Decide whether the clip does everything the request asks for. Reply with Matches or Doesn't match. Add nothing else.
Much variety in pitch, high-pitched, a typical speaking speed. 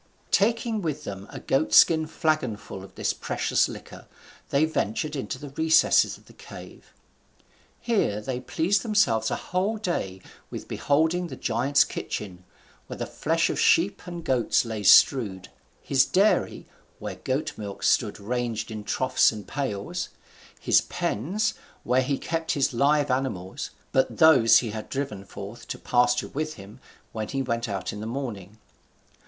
Doesn't match